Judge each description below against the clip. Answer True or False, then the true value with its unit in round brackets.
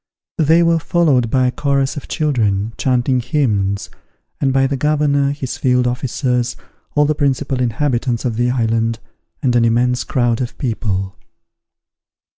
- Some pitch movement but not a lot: True (3.2 semitones)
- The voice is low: True (125 Hz)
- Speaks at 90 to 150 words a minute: True (145 wpm)